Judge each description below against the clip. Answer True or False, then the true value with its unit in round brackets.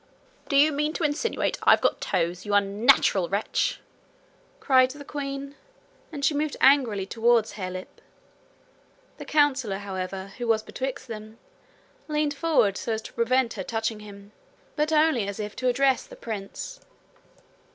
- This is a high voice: True (235 Hz)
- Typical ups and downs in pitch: False (5.8 semitones)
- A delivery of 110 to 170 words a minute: True (150 wpm)